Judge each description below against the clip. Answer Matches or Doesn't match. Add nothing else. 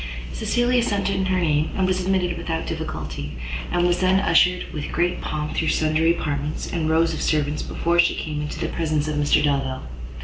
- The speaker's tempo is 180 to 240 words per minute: Matches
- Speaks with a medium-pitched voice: Matches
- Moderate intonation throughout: Matches